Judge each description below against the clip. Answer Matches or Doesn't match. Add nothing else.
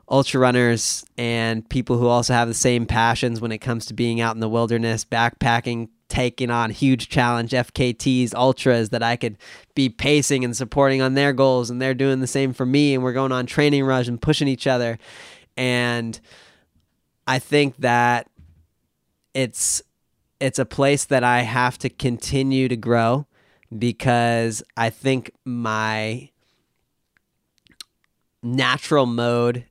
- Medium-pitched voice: Doesn't match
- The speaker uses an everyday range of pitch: Doesn't match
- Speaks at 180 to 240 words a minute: Doesn't match